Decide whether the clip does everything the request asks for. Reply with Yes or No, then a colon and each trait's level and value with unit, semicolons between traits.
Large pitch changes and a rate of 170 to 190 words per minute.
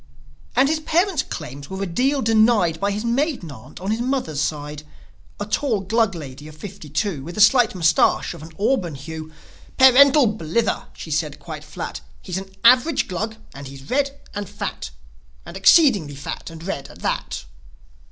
Yes: wide, 7.5 semitones; average, 175 wpm